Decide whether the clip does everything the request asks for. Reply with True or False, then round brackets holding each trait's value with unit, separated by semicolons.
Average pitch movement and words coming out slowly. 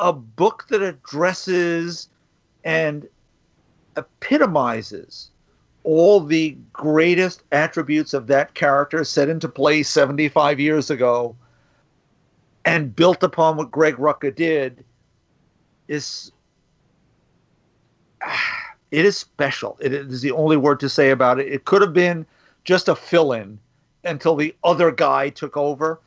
True (3.1 semitones; 125 wpm)